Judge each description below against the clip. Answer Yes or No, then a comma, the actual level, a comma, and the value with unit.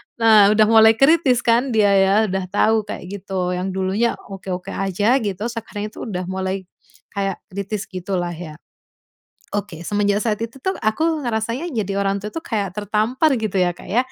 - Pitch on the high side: Yes, high, 205 Hz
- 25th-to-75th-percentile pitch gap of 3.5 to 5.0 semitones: No, average, 2.9 semitones